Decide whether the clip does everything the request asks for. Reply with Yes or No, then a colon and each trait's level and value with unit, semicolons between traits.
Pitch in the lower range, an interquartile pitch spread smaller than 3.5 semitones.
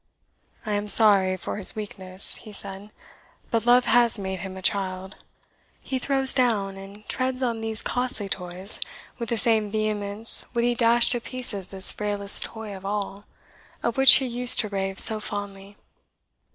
No: high, 210 Hz; average, 3.1 semitones